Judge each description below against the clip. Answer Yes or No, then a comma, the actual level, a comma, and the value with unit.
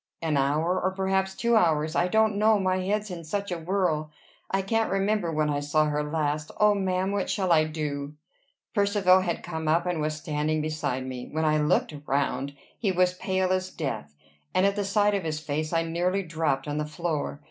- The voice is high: No, medium, 170 Hz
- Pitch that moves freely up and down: No, average, 4.0 semitones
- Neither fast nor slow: No, fast, 210 wpm